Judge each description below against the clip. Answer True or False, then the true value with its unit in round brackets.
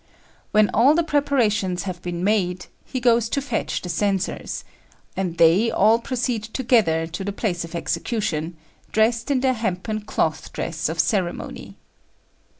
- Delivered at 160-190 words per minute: False (150 wpm)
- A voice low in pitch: False (205 Hz)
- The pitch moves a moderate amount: True (4.9 semitones)